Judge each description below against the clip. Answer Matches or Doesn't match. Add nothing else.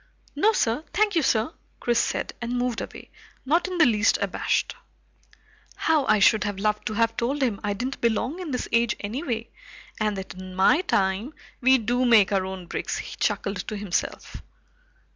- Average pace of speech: Matches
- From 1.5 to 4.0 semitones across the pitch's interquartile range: Doesn't match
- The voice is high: Matches